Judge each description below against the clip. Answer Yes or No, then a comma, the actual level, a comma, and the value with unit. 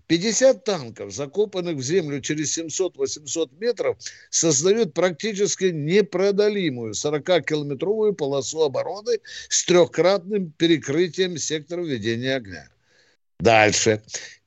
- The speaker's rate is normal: No, slow, 85 wpm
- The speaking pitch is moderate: Yes, medium, 170 Hz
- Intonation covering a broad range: Yes, wide, 6.1 semitones